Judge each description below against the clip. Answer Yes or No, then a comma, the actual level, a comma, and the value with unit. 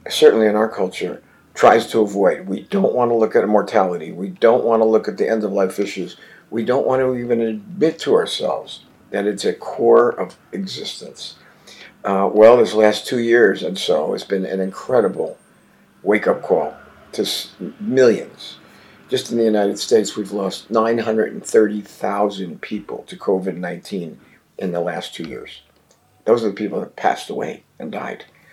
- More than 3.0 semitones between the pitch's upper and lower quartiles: No, narrow, 2.5 semitones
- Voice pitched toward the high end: No, low, 110 Hz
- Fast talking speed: No, average, 175 wpm